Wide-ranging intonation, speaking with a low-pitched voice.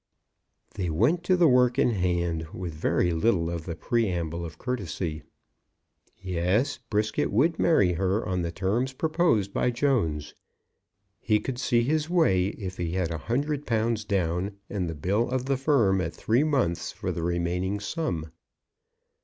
Yes: wide, 6.5 semitones; low, 100 Hz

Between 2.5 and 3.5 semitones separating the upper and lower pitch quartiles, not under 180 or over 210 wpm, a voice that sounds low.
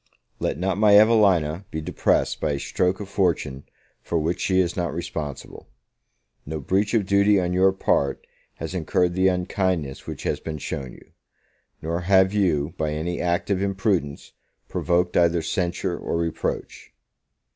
No: average, 3.2 semitones; average, 155 wpm; very low, 90 Hz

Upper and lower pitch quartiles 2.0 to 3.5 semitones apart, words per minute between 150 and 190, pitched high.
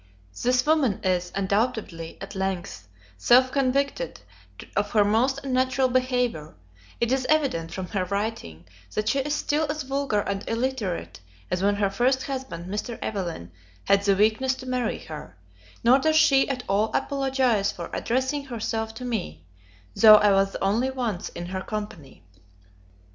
No: average, 5.1 semitones; average, 155 wpm; high, 225 Hz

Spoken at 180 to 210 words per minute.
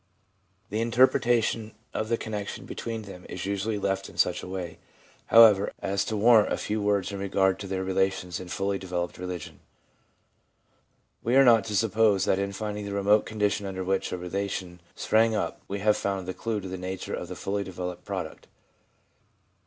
Yes: average, 185 wpm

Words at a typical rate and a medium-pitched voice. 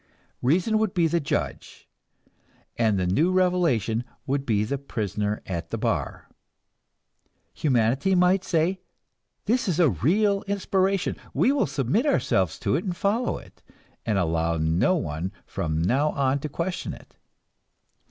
Yes: average, 145 wpm; medium, 145 Hz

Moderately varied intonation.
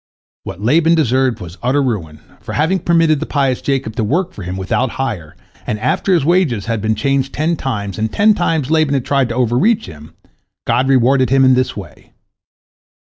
No: wide, 5.9 semitones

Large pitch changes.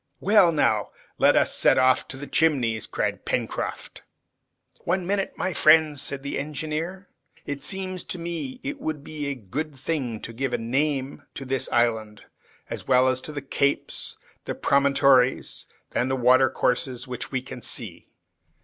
No: average, 3.7 semitones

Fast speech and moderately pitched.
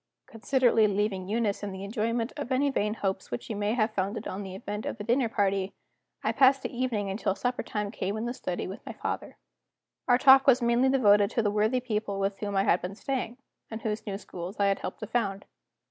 No: fast, 225 wpm; high, 210 Hz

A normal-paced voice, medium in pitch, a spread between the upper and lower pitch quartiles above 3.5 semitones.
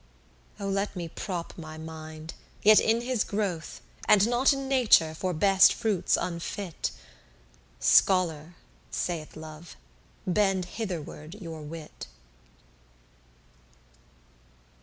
No: slow, 100 wpm; medium, 180 Hz; average, 4.5 semitones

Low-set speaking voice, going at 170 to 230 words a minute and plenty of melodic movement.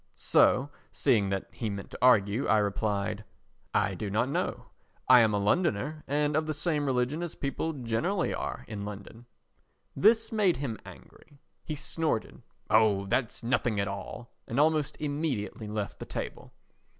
No: low, 125 Hz; average, 160 wpm; wide, 6.2 semitones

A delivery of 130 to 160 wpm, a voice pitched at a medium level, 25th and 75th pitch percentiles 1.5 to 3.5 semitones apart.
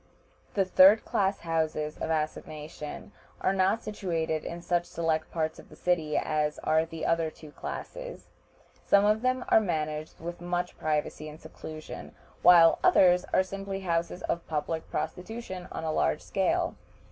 Yes: average, 155 wpm; medium, 165 Hz; average, 3.2 semitones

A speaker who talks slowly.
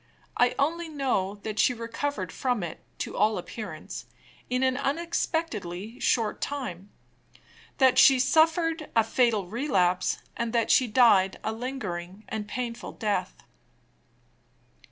Yes: slow, 130 wpm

